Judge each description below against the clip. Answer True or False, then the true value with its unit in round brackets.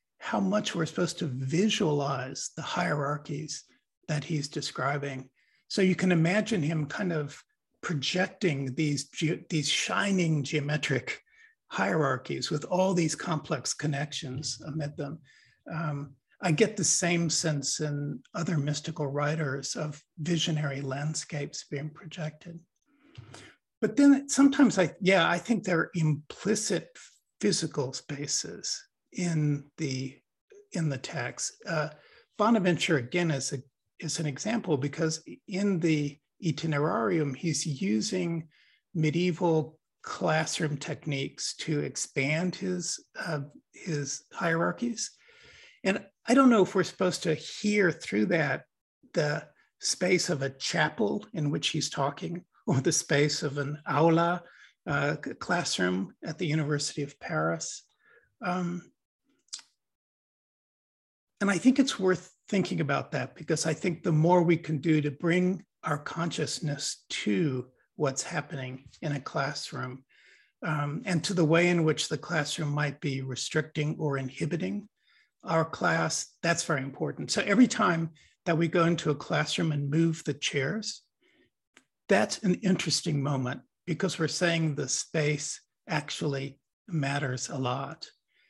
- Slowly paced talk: True (130 wpm)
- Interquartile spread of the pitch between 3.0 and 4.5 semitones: True (3.6 semitones)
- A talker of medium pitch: True (160 Hz)